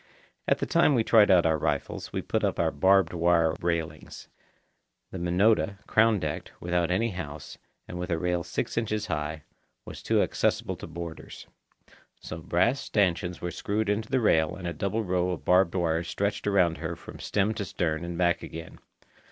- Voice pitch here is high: No, very low, 90 Hz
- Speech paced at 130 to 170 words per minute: No, average, 185 wpm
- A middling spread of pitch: Yes, average, 3.4 semitones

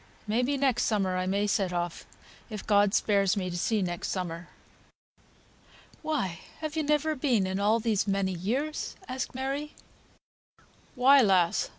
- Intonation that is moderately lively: No, wide, 5.9 semitones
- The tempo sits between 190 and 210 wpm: No, average, 155 wpm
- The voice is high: Yes, high, 210 Hz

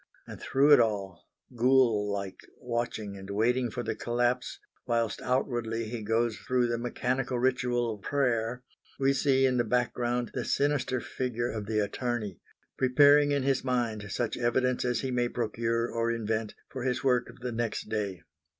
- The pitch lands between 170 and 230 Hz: No, low, 120 Hz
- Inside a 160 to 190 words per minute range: Yes, average, 170 wpm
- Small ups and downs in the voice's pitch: Yes, narrow, 2.2 semitones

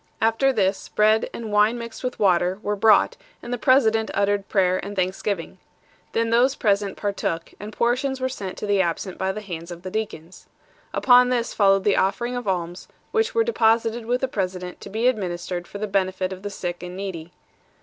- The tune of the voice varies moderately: Yes, average, 3.7 semitones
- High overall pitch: Yes, high, 205 Hz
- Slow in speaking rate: No, average, 195 wpm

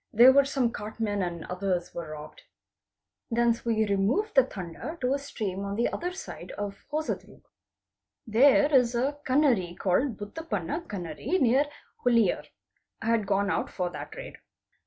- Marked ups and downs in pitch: Yes, wide, 5.7 semitones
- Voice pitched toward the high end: Yes, high, 230 Hz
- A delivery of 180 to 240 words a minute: No, average, 150 wpm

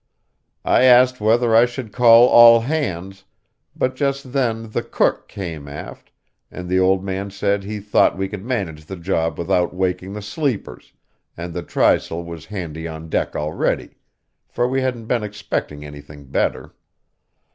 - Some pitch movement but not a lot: No, wide, 5.7 semitones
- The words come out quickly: No, average, 155 wpm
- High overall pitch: No, low, 100 Hz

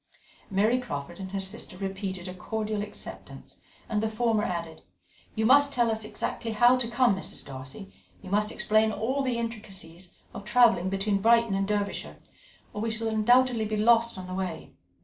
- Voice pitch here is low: No, high, 210 Hz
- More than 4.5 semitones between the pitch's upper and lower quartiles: No, average, 3.3 semitones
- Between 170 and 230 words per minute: Yes, average, 175 wpm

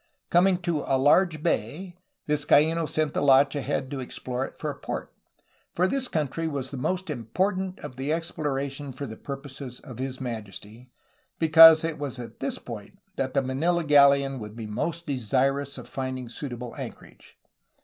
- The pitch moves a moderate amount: Yes, average, 3.7 semitones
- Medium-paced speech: Yes, average, 170 wpm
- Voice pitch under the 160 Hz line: Yes, medium, 140 Hz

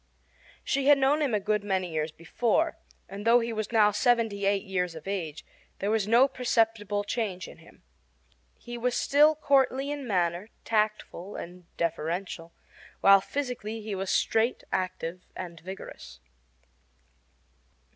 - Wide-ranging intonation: No, average, 4.5 semitones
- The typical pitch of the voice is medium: No, high, 210 Hz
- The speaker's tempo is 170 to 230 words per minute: No, average, 145 wpm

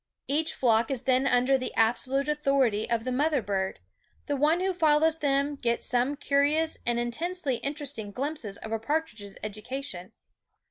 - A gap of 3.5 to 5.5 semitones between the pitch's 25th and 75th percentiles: Yes, average, 4.2 semitones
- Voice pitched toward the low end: No, very high, 270 Hz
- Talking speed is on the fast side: No, average, 165 wpm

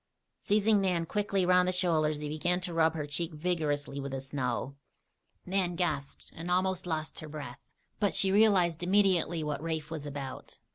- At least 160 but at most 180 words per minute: Yes, average, 175 wpm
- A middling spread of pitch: Yes, average, 3.4 semitones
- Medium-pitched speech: Yes, medium, 165 Hz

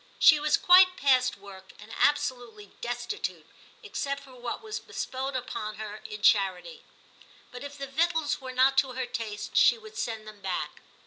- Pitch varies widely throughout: No, average, 4.7 semitones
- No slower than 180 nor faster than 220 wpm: No, average, 170 wpm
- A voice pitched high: Yes, very high, 250 Hz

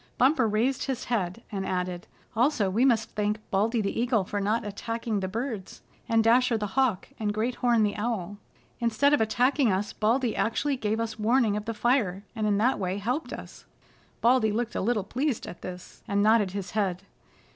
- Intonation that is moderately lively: Yes, average, 3.0 semitones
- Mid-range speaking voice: No, high, 220 Hz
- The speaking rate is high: No, average, 190 wpm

